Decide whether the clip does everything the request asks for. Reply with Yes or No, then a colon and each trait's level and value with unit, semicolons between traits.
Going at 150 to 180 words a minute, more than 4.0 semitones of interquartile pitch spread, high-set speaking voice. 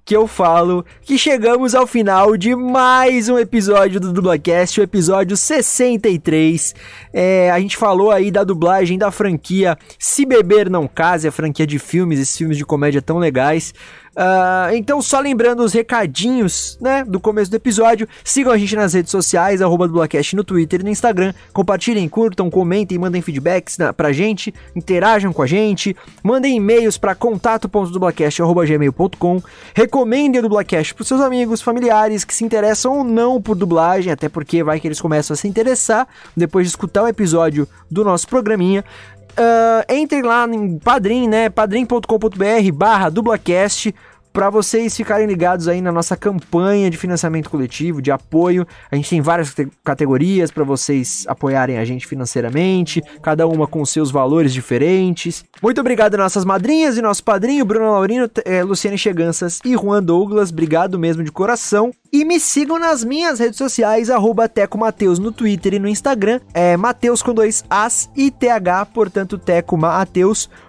Yes: average, 160 wpm; average, 5.0 semitones; high, 195 Hz